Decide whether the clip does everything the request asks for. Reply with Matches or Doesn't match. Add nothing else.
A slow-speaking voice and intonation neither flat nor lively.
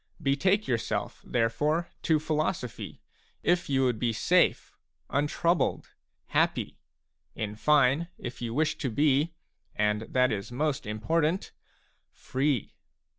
Matches